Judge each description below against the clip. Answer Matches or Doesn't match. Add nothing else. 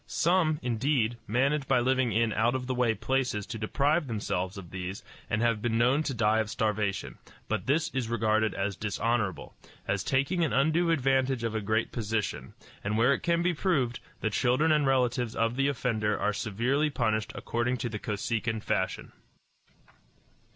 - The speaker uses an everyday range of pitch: Matches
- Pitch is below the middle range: Matches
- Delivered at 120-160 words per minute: Doesn't match